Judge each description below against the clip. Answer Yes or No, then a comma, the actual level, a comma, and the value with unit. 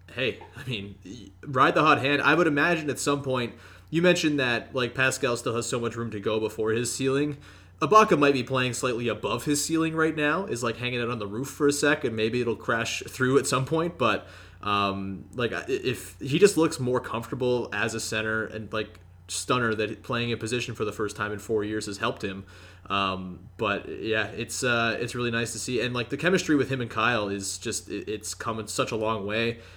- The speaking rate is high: Yes, fast, 225 wpm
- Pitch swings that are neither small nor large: Yes, average, 4.0 semitones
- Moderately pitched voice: No, low, 115 Hz